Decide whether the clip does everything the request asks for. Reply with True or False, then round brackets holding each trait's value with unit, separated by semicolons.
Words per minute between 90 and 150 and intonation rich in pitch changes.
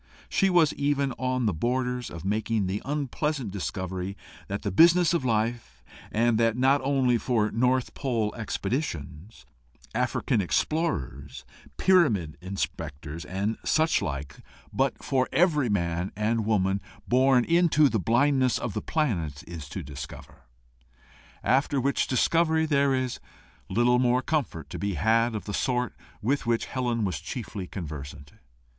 True (140 wpm; 5.9 semitones)